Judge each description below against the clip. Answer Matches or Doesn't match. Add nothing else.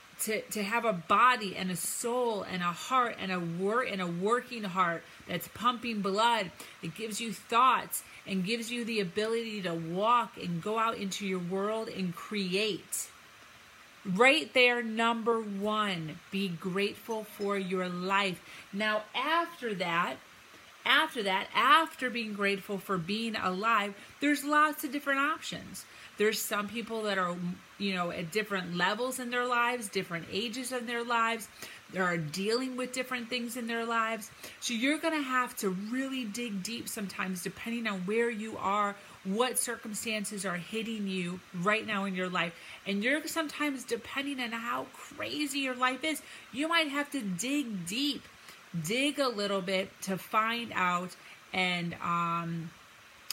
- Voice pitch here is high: Matches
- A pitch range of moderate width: Matches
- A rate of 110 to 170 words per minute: Matches